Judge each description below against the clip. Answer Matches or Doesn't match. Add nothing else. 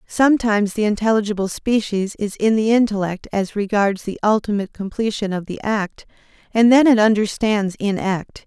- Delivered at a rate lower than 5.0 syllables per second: Doesn't match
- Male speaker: Doesn't match